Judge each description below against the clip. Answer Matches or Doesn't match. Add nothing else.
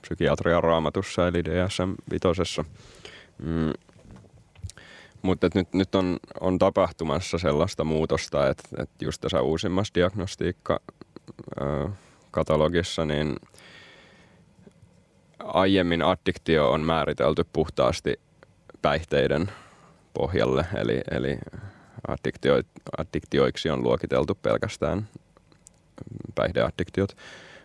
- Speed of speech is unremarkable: Doesn't match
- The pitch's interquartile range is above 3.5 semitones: Doesn't match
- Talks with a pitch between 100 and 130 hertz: Doesn't match